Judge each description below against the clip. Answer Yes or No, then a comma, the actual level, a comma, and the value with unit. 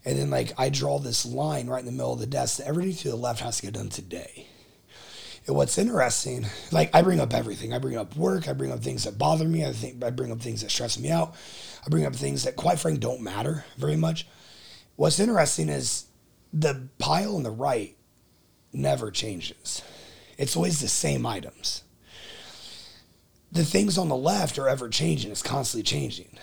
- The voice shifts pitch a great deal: Yes, wide, 5.9 semitones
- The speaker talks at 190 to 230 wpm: Yes, fast, 205 wpm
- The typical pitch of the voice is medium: No, low, 130 Hz